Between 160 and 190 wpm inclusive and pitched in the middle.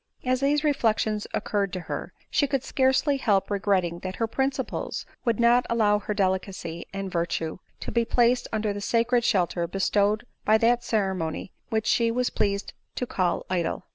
No: average, 170 wpm; high, 215 Hz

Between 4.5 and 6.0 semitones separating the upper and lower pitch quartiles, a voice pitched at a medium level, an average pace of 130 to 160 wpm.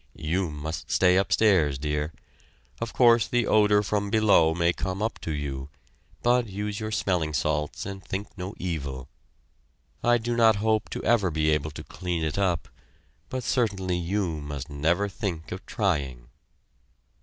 No: average, 5.3 semitones; very low, 95 Hz; average, 155 wpm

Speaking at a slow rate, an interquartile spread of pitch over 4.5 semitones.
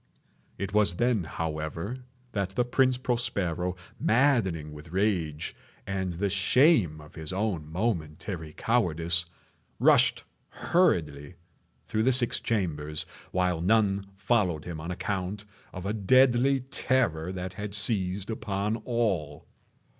Yes: slow, 120 wpm; average, 5.3 semitones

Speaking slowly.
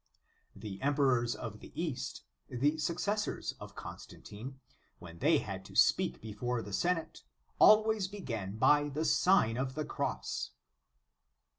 Yes: slow, 130 wpm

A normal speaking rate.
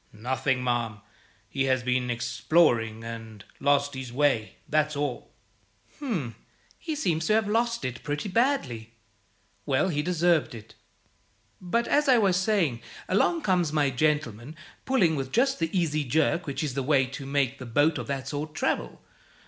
Yes: average, 160 wpm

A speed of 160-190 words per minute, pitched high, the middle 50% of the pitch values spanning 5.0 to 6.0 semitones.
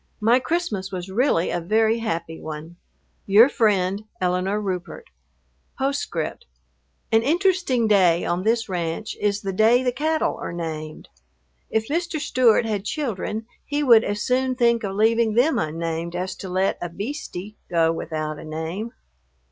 No: average, 150 wpm; high, 210 Hz; wide, 5.6 semitones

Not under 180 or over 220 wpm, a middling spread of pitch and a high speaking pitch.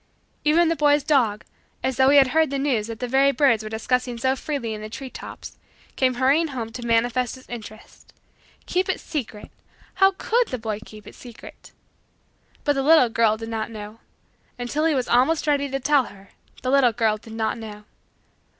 Yes: average, 195 wpm; average, 4.1 semitones; very high, 255 Hz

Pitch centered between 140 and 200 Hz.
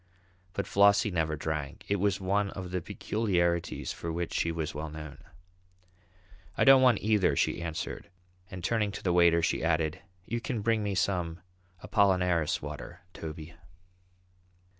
No: very low, 90 Hz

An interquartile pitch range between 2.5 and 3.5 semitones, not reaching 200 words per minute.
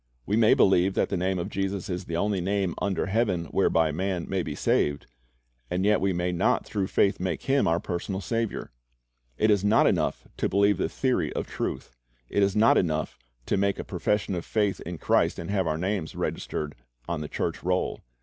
No: average, 2.8 semitones; fast, 205 wpm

